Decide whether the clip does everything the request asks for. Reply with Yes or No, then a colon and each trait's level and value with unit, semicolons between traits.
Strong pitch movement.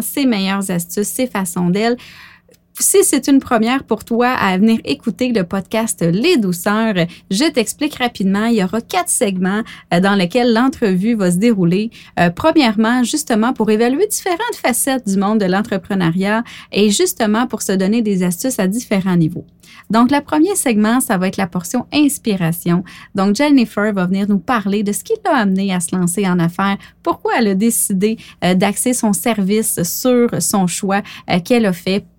No: average, 4.1 semitones